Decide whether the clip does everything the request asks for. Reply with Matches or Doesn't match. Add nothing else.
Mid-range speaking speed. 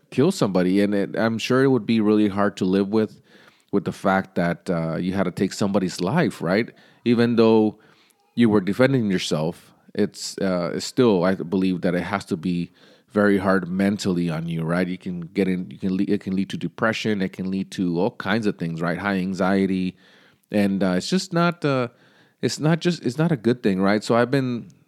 Doesn't match